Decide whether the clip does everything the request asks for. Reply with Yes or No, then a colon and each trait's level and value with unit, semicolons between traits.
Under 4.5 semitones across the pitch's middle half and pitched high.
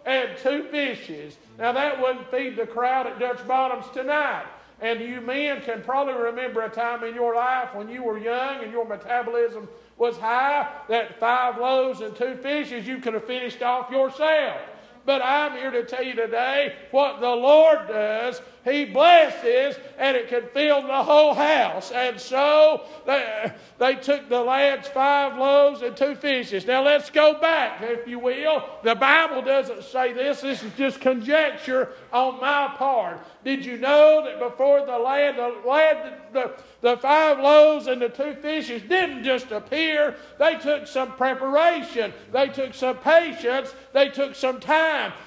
Yes: average, 2.8 semitones; very high, 260 Hz